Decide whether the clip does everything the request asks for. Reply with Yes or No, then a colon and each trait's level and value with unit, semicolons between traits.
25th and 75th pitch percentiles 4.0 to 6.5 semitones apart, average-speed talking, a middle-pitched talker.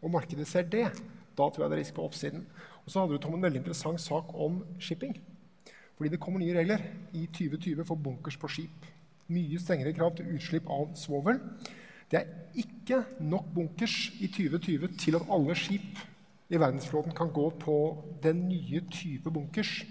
No: average, 3.3 semitones; average, 185 wpm; medium, 170 Hz